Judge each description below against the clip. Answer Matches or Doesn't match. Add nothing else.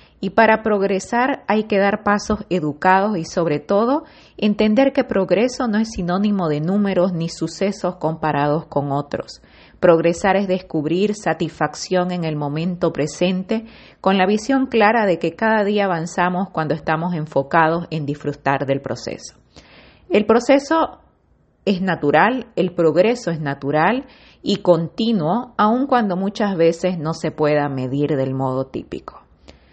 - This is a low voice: Doesn't match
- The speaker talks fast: Doesn't match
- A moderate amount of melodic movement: Matches